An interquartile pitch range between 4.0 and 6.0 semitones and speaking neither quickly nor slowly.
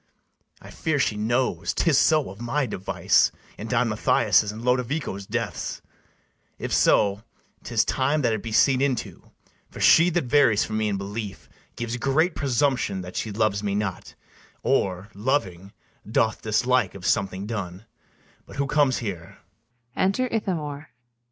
Yes: average, 5.0 semitones; average, 145 wpm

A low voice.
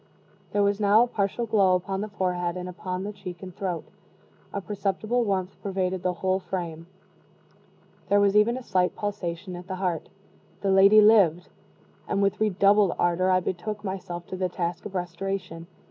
No: high, 190 Hz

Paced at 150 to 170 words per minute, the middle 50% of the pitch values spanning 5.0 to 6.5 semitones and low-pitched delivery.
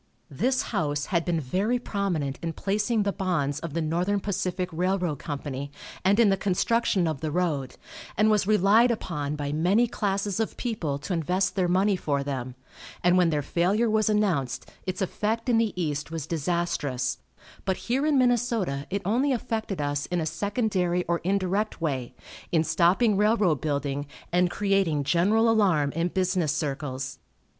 No: average, 165 wpm; wide, 5.4 semitones; medium, 180 Hz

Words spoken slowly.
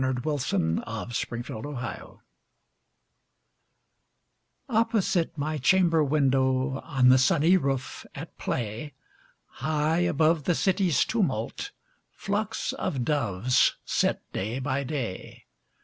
Yes: slow, 100 wpm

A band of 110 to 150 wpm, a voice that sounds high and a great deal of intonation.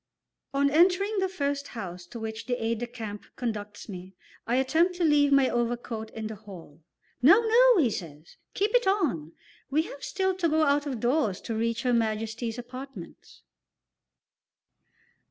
No: average, 165 wpm; high, 245 Hz; wide, 6.1 semitones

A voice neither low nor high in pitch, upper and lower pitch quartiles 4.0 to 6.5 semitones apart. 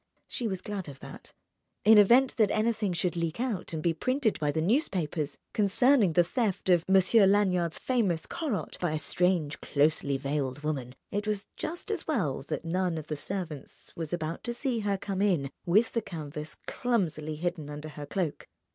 Yes: medium, 180 Hz; wide, 5.4 semitones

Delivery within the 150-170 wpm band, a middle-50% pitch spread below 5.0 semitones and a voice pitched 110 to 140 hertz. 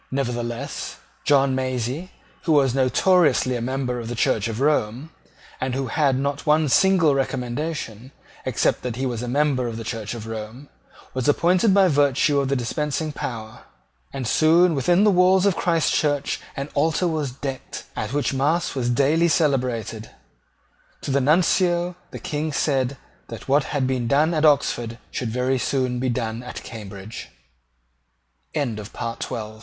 Yes: average, 155 wpm; average, 3.9 semitones; low, 135 Hz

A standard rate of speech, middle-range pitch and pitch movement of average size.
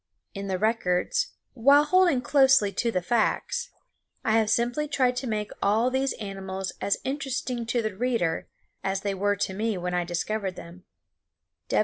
No: average, 160 wpm; high, 220 Hz; average, 4.9 semitones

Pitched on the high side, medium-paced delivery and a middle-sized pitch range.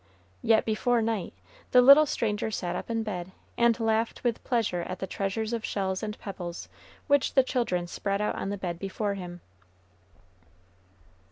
Yes: high, 210 Hz; average, 165 wpm; average, 3.4 semitones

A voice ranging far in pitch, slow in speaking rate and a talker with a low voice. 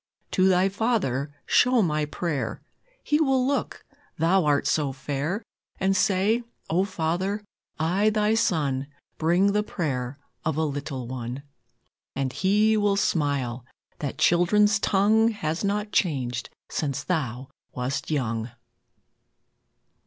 No: wide, 6.7 semitones; slow, 125 wpm; medium, 170 Hz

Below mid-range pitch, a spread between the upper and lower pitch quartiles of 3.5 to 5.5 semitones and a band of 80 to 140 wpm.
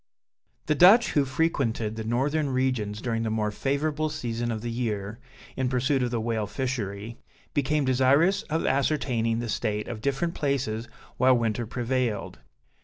No: low, 125 Hz; average, 3.8 semitones; average, 155 wpm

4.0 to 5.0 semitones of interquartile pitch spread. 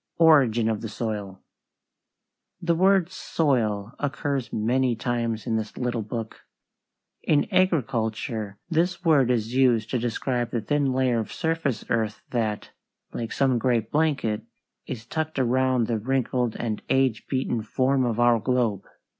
No: average, 3.5 semitones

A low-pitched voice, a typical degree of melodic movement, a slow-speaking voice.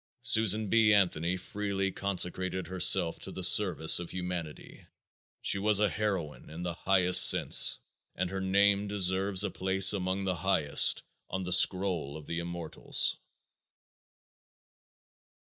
No: very low, 95 Hz; narrow, 2.1 semitones; slow, 130 wpm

